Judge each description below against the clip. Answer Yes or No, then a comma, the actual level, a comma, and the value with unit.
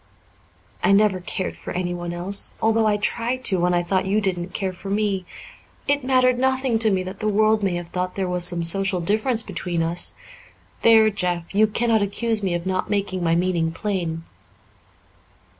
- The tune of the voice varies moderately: Yes, average, 3.5 semitones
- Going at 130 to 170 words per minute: No, average, 185 wpm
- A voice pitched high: Yes, high, 195 Hz